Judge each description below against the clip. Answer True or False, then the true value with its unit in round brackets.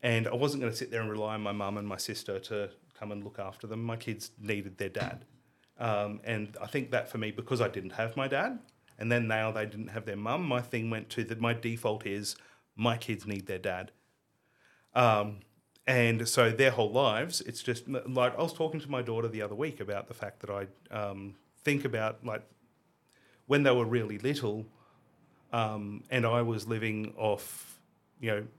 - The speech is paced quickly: True (210 wpm)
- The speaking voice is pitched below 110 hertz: False (115 Hz)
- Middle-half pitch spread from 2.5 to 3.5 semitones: True (2.8 semitones)